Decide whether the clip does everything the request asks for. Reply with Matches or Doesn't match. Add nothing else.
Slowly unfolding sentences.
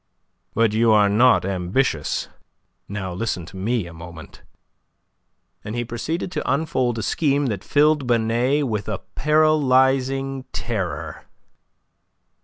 Matches